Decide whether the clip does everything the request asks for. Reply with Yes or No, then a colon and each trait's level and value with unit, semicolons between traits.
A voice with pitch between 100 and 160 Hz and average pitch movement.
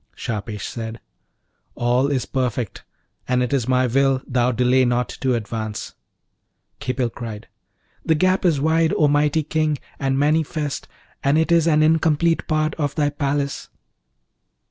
Yes: medium, 140 Hz; average, 3.7 semitones